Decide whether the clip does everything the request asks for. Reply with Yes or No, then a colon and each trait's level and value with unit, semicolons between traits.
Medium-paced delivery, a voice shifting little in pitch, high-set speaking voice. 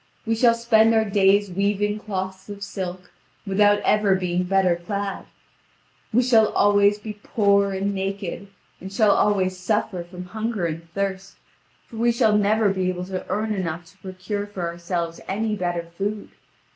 Yes: average, 160 wpm; narrow, 2.3 semitones; high, 200 Hz